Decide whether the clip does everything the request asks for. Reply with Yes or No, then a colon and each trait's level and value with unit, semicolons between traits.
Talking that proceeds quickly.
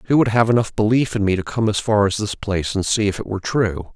Yes: fast, 305 wpm